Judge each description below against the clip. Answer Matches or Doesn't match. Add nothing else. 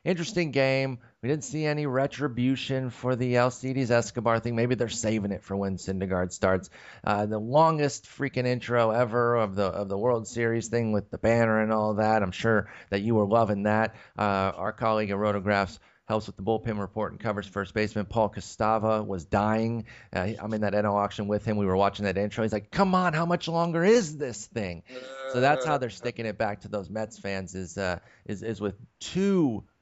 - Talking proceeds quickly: Matches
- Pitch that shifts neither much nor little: Matches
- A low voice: Matches